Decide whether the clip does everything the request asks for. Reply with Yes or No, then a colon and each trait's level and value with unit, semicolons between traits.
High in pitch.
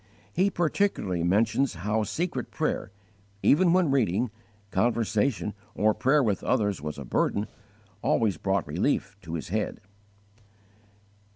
No: low, 110 Hz